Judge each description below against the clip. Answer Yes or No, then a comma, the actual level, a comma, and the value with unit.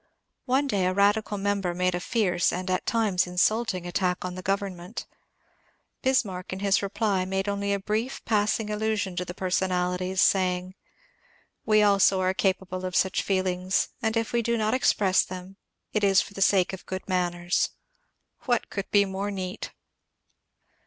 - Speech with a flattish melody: Yes, narrow, 2.2 semitones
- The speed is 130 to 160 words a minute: No, average, 175 wpm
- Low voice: No, high, 195 Hz